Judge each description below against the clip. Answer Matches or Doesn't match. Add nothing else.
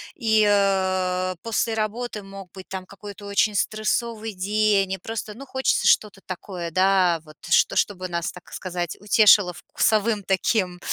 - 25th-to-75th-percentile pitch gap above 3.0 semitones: Doesn't match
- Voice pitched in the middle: Doesn't match